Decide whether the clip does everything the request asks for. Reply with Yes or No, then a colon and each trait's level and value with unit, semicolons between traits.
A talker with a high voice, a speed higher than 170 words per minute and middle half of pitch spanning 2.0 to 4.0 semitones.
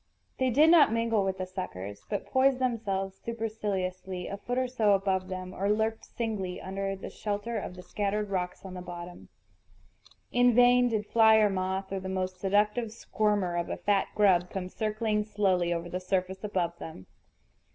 Yes: high, 195 Hz; average, 180 wpm; average, 3.0 semitones